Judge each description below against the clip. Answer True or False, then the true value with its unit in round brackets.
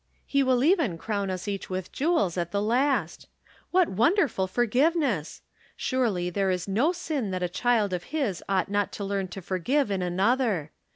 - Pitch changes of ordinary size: False (6.0 semitones)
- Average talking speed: True (175 wpm)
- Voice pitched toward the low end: False (205 Hz)